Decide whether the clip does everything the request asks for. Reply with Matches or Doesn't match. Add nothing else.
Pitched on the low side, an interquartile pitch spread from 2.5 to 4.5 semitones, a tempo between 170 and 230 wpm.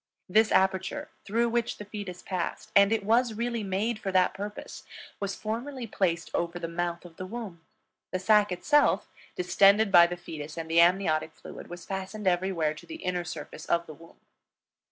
Doesn't match